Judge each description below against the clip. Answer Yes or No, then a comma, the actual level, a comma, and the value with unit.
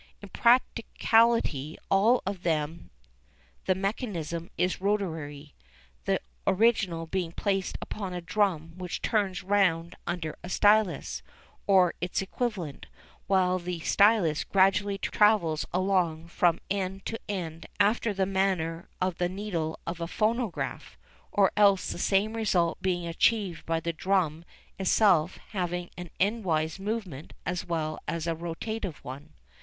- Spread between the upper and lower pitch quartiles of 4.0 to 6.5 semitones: No, average, 3.4 semitones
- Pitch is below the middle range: No, medium, 185 Hz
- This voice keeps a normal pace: No, slow, 130 wpm